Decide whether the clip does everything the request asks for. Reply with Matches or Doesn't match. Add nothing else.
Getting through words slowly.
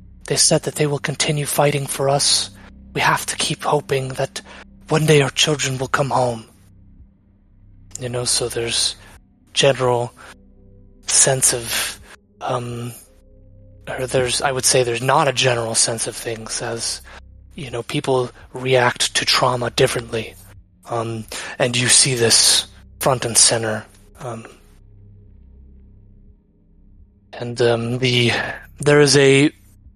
Matches